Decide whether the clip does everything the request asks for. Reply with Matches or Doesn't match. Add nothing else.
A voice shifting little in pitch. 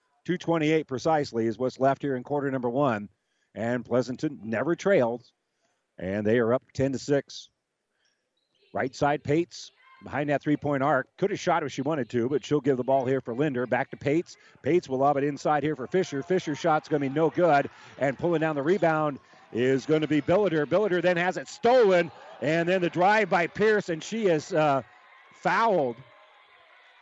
Doesn't match